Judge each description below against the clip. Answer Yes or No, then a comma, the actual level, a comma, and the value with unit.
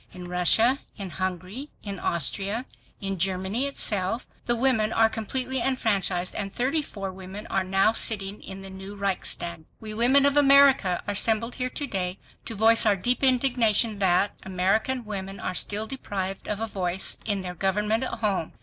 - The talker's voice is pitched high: Yes, high, 205 Hz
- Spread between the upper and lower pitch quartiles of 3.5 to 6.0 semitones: Yes, average, 3.8 semitones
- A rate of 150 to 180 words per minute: Yes, average, 170 wpm